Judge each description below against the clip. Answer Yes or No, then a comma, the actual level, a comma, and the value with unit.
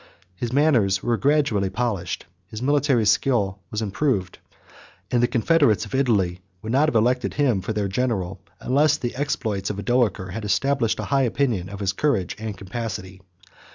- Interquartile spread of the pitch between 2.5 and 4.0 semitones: No, average, 5.1 semitones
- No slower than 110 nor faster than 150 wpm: No, average, 165 wpm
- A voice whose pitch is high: No, low, 115 Hz